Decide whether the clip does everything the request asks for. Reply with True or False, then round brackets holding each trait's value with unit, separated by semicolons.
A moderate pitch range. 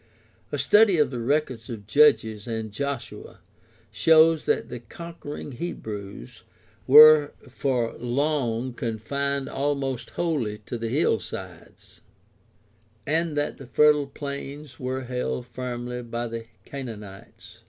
True (4.0 semitones)